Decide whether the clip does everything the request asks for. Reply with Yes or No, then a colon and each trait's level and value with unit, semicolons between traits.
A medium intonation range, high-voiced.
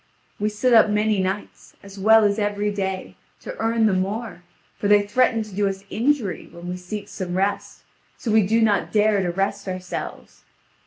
No: narrow, 2.2 semitones; high, 205 Hz